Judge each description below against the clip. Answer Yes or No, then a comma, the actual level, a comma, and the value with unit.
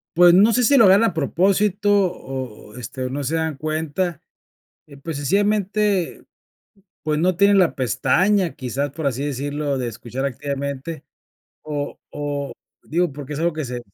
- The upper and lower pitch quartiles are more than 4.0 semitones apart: Yes, average, 5.0 semitones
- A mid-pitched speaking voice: Yes, medium, 155 Hz